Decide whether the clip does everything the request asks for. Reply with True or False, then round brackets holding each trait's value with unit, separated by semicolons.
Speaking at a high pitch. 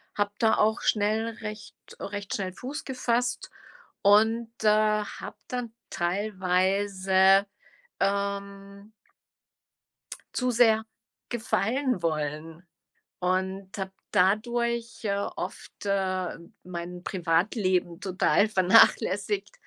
True (200 Hz)